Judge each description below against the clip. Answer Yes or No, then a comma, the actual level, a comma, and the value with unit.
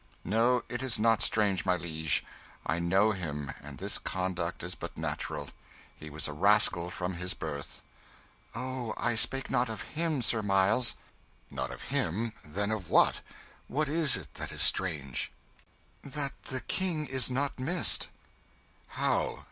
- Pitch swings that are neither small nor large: No, wide, 6.8 semitones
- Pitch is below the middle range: Yes, low, 105 Hz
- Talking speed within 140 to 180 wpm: Yes, average, 155 wpm